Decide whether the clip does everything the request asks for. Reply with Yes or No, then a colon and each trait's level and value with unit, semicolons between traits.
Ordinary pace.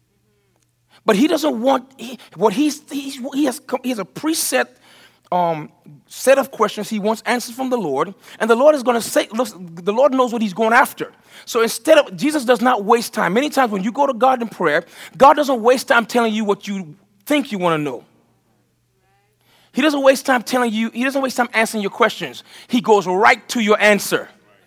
No: fast, 215 wpm